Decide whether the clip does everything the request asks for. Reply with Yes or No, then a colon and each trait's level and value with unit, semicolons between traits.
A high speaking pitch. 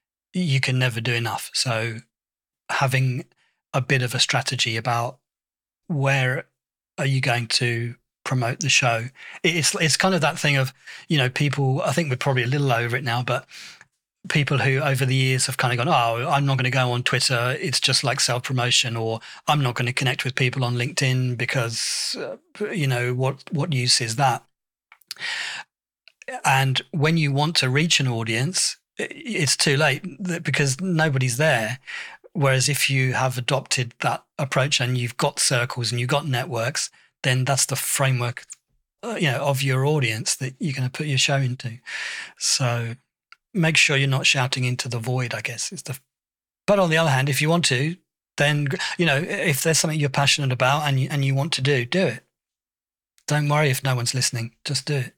No: low, 135 Hz